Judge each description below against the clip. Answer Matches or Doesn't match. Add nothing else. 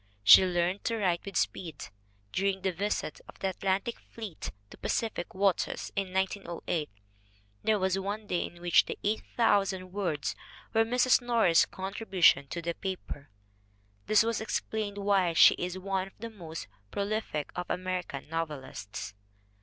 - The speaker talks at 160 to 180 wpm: Doesn't match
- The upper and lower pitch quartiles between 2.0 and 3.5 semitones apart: Matches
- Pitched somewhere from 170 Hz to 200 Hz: Matches